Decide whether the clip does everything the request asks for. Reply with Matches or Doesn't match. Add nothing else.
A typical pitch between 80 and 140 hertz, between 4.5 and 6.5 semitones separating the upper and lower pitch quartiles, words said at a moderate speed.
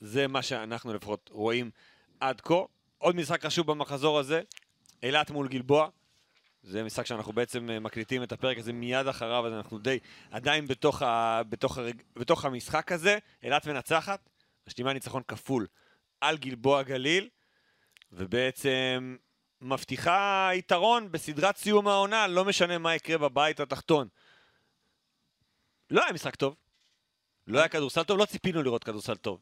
Matches